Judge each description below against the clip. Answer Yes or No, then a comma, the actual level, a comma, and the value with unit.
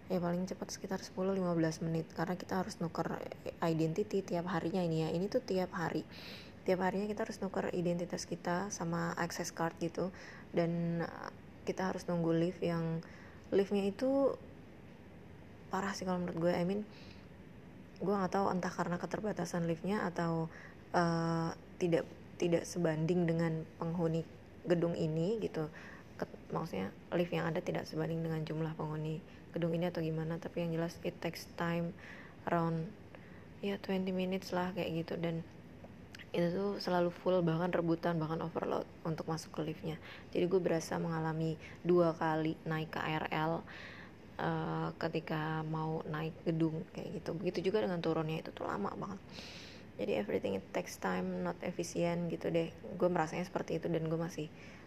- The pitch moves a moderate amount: No, narrow, 1.8 semitones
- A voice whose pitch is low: No, medium, 170 Hz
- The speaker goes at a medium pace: No, fast, 155 wpm